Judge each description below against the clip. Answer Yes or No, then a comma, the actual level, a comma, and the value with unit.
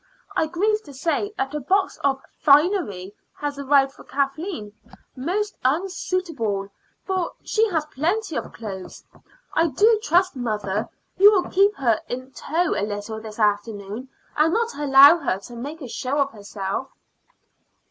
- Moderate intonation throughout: No, wide, 7.9 semitones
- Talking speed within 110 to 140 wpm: No, average, 150 wpm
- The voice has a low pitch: No, very high, 280 Hz